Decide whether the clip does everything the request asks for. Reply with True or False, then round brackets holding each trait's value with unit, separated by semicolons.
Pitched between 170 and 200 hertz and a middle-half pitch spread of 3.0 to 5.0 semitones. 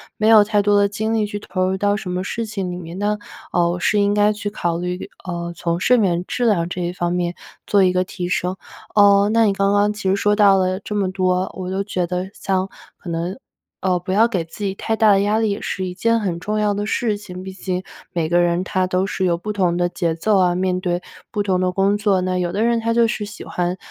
False (190 Hz; 2.4 semitones)